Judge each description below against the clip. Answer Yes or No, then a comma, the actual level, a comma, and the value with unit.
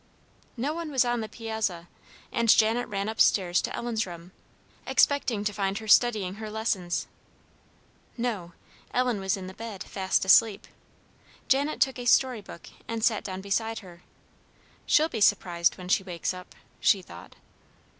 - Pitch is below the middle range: No, high, 215 Hz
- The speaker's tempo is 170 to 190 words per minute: No, average, 160 wpm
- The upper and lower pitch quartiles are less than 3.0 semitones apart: No, average, 3.8 semitones